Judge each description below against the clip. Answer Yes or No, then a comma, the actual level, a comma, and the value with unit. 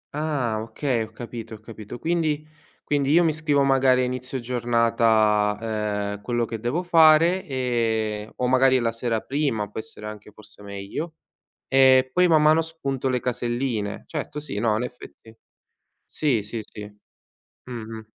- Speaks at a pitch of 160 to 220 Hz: No, low, 125 Hz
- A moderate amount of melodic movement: Yes, average, 4.6 semitones